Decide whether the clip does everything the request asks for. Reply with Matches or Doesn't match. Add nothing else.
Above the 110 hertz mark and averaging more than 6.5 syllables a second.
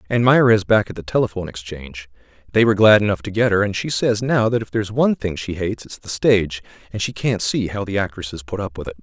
Doesn't match